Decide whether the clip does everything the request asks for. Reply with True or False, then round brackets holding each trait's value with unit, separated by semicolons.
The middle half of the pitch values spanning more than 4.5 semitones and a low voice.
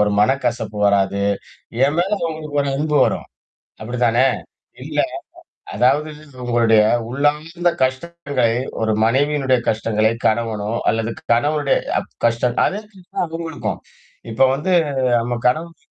True (5.1 semitones; 130 Hz)